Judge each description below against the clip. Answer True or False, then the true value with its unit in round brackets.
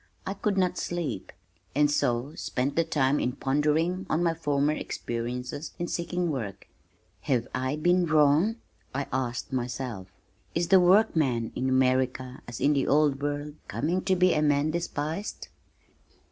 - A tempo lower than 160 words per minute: True (150 wpm)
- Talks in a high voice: False (145 Hz)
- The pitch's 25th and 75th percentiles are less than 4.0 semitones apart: False (4.5 semitones)